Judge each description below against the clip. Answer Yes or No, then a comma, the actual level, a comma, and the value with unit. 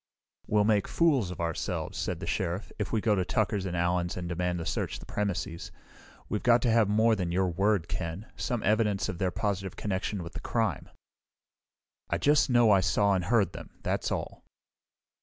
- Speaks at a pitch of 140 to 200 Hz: No, very low, 95 Hz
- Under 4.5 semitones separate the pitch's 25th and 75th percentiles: Yes, average, 3.5 semitones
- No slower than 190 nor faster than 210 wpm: Yes, average, 195 wpm